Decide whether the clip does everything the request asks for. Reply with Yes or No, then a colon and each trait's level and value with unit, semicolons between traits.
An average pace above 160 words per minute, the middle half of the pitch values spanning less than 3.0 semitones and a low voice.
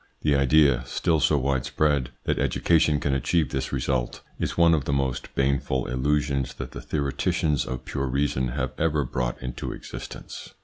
Yes: average, 170 wpm; narrow, 2.5 semitones; very low, 70 Hz